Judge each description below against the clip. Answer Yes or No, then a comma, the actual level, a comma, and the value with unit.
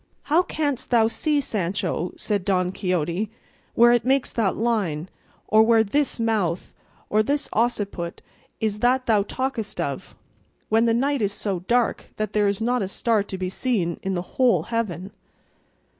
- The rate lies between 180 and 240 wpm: No, average, 165 wpm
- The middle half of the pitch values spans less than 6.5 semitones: Yes, average, 4.0 semitones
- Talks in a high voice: Yes, high, 215 Hz